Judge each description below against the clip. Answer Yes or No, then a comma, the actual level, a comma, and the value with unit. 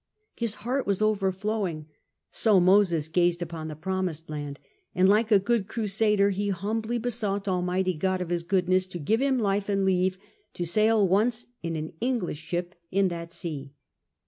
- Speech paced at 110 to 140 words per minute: No, average, 175 wpm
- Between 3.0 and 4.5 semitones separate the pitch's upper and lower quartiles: Yes, average, 3.5 semitones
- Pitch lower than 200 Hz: Yes, high, 190 Hz